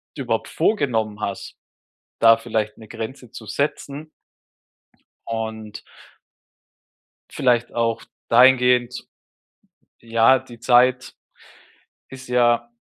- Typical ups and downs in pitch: No, narrow, 2.1 semitones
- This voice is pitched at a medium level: No, low, 120 Hz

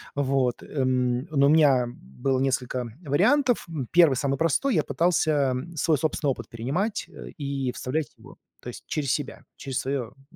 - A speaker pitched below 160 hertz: Yes, medium, 140 Hz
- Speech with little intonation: No, average, 3.5 semitones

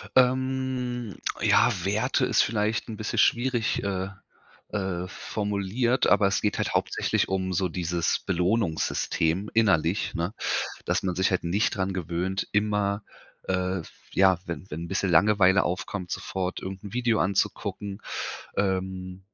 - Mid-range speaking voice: No, very low, 95 Hz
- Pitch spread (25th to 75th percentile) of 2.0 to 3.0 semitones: Yes, narrow, 2.6 semitones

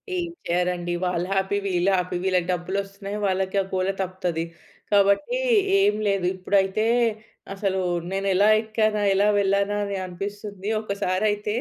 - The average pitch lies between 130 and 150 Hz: No, high, 195 Hz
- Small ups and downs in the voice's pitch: Yes, narrow, 1.7 semitones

